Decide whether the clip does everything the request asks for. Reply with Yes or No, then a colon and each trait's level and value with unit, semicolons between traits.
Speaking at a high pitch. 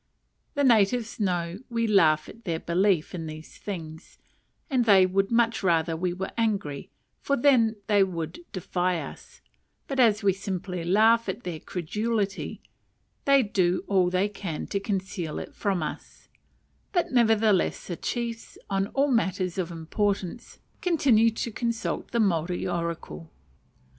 Yes: high, 195 Hz